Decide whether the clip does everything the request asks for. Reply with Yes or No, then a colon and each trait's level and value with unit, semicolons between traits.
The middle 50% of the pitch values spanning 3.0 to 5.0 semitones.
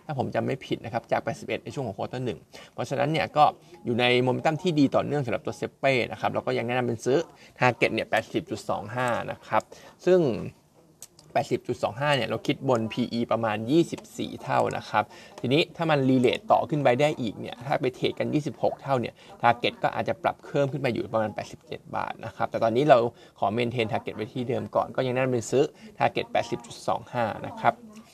Yes: average, 4.2 semitones